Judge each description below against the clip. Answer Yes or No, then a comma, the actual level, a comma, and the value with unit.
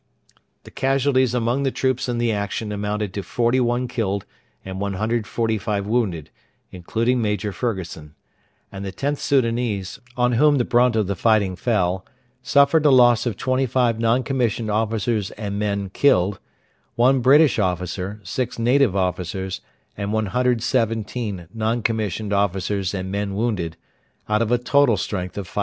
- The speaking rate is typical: Yes, average, 145 wpm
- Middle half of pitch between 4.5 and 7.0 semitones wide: No, average, 3.7 semitones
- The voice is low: Yes, low, 110 Hz